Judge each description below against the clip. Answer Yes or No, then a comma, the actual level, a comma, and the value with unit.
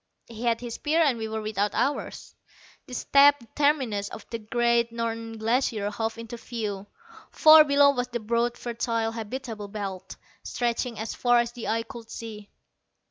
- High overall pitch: Yes, high, 230 Hz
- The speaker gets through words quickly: No, average, 165 wpm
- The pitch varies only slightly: Yes, narrow, 1.9 semitones